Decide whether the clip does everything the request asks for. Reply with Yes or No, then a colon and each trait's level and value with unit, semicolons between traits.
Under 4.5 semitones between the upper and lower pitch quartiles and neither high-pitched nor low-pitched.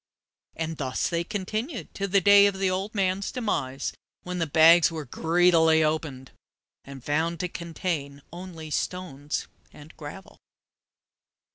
Yes: average, 3.7 semitones; medium, 170 Hz